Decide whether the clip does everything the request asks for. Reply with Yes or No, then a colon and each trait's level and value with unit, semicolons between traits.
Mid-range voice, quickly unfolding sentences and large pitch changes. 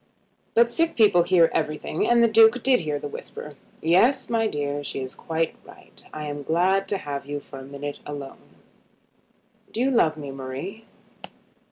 No: medium, 160 Hz; average, 175 wpm; wide, 7.5 semitones